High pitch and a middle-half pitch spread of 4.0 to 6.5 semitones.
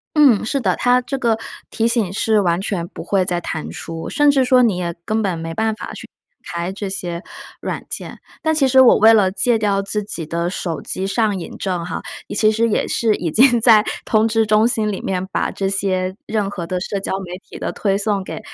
No: high, 205 Hz; average, 3.5 semitones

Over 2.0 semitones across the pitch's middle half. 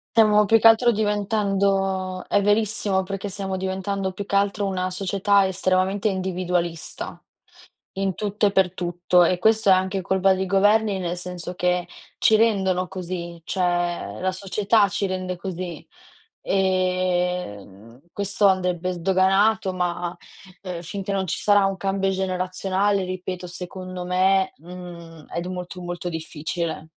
No: narrow, 1.7 semitones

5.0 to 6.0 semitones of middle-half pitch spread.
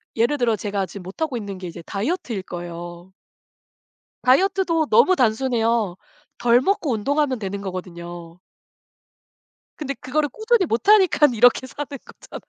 No: wide, 7.5 semitones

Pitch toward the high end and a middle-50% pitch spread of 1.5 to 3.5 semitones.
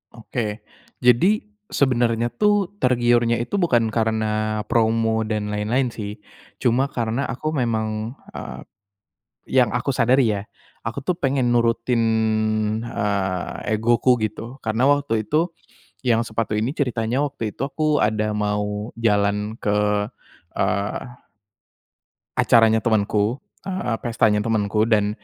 No: low, 115 Hz; narrow, 2.4 semitones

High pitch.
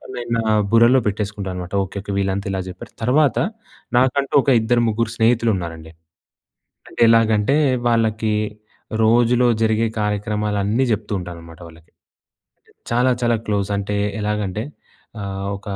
No: low, 105 Hz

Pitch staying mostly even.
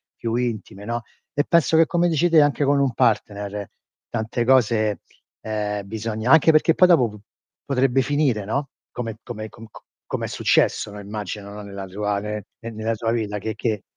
No: average, 4.3 semitones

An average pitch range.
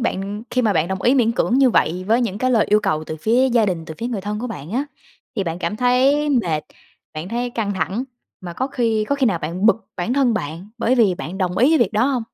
Yes: average, 5.0 semitones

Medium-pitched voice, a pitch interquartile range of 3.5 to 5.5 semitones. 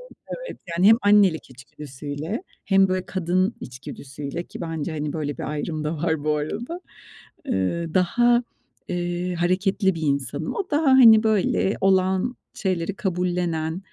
Yes: medium, 175 Hz; average, 4.1 semitones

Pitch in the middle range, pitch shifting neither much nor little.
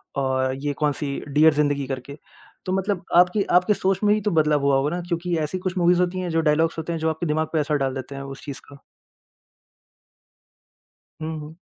Yes: medium, 155 Hz; average, 3.8 semitones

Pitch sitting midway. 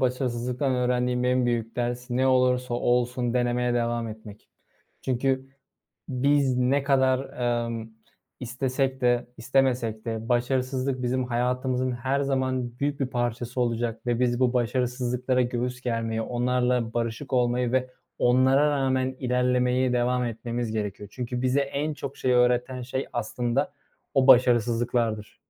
No: low, 125 Hz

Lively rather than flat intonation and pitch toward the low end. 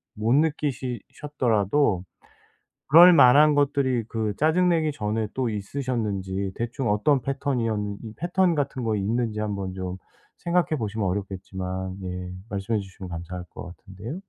Yes: wide, 6.4 semitones; low, 115 Hz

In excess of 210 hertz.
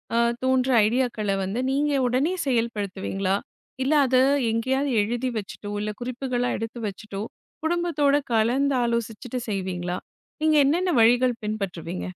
Yes: high, 240 Hz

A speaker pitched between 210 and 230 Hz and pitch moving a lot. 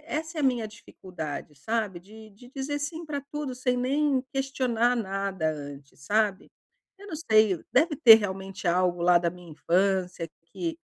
Yes: high, 215 Hz; wide, 7.0 semitones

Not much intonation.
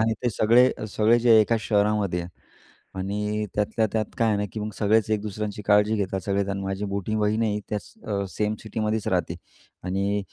Yes: narrow, 1.4 semitones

